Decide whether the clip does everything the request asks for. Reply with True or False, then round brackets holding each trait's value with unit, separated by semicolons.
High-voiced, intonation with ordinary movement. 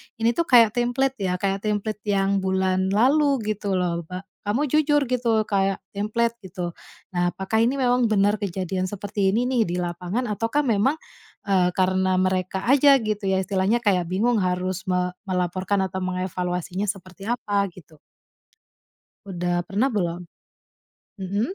True (195 Hz; 3.6 semitones)